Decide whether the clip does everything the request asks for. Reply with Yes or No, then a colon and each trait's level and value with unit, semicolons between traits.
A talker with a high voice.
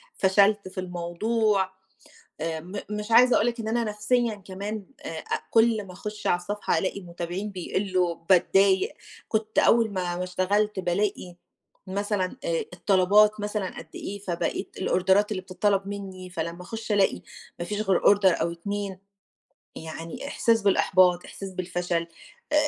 Yes: high, 195 Hz